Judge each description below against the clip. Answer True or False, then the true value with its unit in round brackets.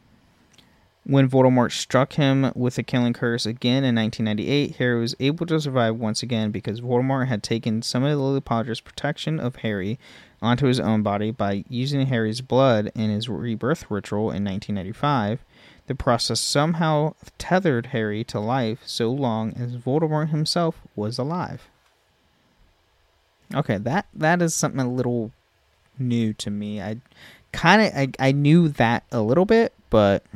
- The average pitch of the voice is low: True (120 Hz)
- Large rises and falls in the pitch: False (4.1 semitones)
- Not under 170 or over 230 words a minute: False (155 wpm)